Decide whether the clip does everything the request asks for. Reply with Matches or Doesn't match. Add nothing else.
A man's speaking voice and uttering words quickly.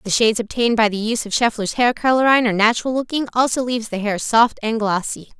Doesn't match